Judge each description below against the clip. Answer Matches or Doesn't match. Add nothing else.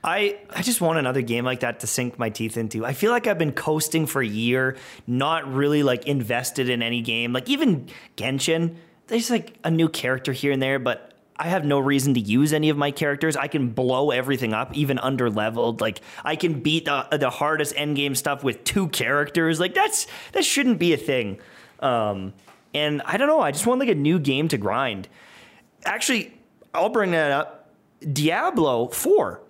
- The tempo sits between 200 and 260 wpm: Matches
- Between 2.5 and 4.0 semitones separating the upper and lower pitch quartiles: Doesn't match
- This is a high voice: Doesn't match